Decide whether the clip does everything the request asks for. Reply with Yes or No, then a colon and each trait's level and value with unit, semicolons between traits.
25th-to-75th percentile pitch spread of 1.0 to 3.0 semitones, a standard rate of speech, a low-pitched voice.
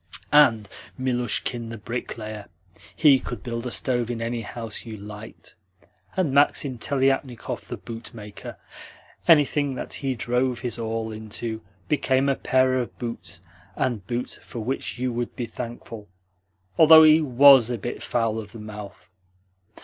Yes: average, 2.7 semitones; average, 145 wpm; low, 120 Hz